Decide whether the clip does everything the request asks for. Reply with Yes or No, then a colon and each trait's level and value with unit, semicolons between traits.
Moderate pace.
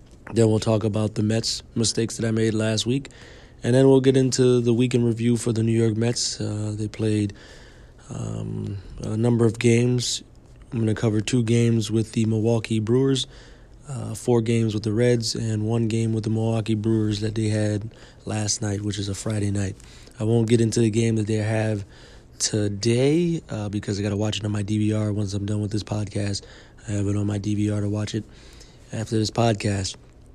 No: fast, 210 wpm